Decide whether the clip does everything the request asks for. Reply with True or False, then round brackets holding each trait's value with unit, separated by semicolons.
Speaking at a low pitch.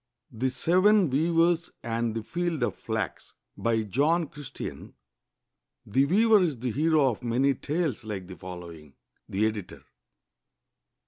True (130 Hz)